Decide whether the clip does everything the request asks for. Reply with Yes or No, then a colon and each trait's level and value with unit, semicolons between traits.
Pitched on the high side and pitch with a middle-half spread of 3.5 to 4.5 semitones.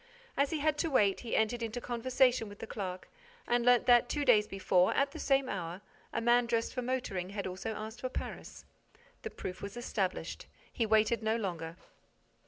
Yes: high, 230 Hz; average, 3.8 semitones